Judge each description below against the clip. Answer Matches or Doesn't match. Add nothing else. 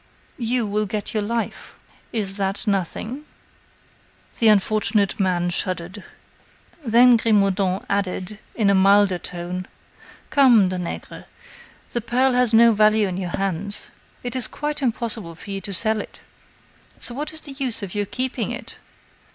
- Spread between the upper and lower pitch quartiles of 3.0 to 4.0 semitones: Matches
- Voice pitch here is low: Doesn't match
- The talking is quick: Doesn't match